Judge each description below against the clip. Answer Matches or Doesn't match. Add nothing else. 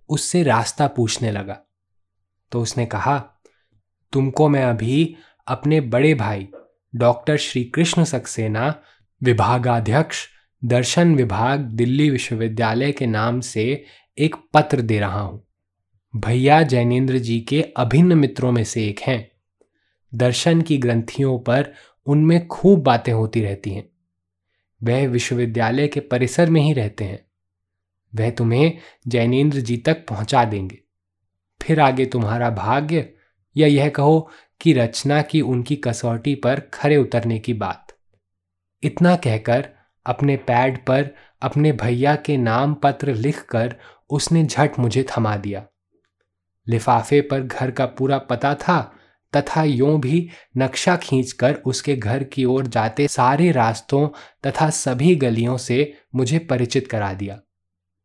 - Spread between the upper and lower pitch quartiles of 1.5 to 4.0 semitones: Doesn't match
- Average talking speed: Matches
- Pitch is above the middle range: Doesn't match